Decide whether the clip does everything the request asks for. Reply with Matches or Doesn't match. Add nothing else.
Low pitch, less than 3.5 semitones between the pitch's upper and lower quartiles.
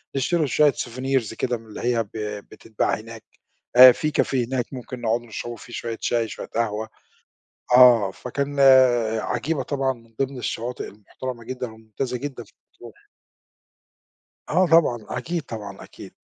Matches